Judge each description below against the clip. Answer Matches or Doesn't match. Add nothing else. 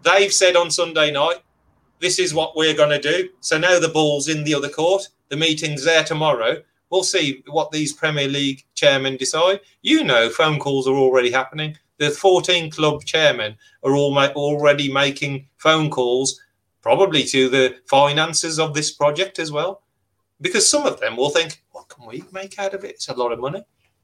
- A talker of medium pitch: Matches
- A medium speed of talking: Matches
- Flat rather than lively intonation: Doesn't match